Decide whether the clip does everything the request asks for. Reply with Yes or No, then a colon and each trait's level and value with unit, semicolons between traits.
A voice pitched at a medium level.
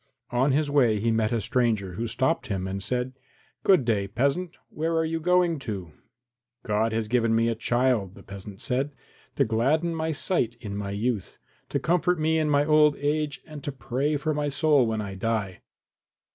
No: low, 125 Hz